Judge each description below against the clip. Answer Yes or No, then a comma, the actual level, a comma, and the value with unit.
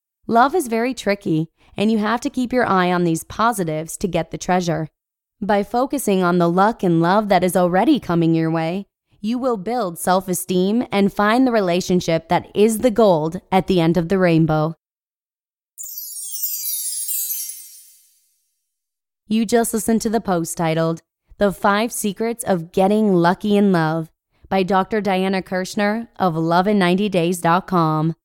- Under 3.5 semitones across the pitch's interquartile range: No, average, 4.3 semitones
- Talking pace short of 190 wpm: Yes, average, 150 wpm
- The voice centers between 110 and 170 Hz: No, medium, 185 Hz